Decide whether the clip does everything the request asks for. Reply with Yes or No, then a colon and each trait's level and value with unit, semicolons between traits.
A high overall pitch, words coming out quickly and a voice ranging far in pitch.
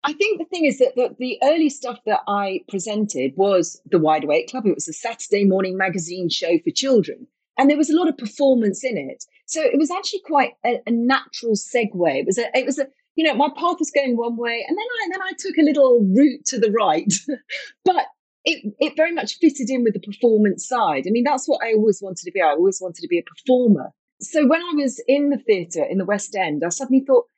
Yes: very high, 255 Hz; fast, 250 wpm; wide, 6.7 semitones